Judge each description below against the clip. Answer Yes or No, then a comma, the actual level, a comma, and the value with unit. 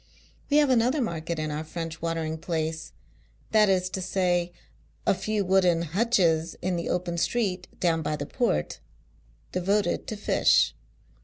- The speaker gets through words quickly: No, average, 160 wpm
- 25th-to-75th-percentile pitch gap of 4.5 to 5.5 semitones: No, average, 3.3 semitones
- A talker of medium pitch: Yes, medium, 175 Hz